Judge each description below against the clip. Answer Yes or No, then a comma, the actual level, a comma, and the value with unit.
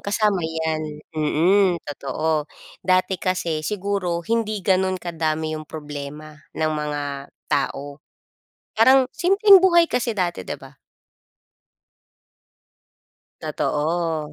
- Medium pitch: Yes, medium, 170 Hz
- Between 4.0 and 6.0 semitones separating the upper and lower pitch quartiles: Yes, average, 4.7 semitones